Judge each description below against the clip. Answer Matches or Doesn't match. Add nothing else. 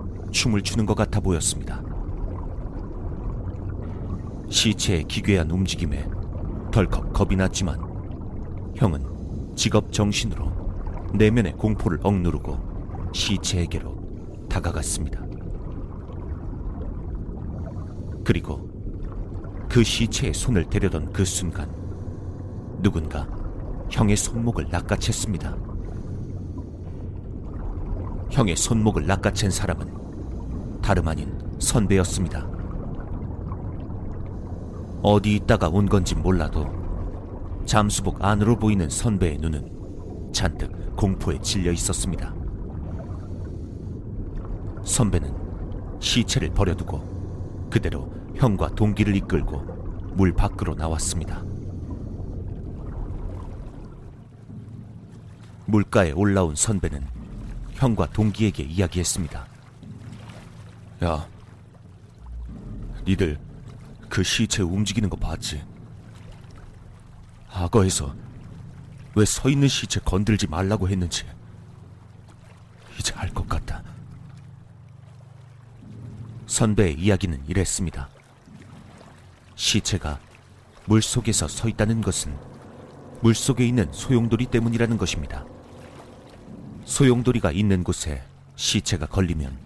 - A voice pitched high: Doesn't match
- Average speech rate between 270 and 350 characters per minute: Doesn't match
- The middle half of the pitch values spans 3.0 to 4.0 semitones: Matches